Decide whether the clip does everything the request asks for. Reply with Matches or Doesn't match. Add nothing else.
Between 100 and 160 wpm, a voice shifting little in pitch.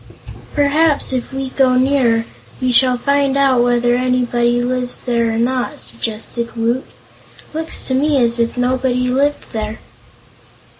Matches